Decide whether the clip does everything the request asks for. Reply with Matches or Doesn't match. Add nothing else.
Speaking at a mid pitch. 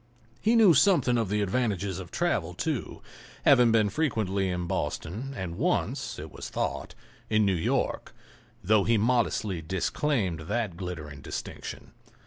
Doesn't match